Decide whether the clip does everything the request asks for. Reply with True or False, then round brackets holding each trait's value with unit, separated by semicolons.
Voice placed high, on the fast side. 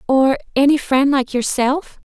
False (270 Hz; 110 wpm)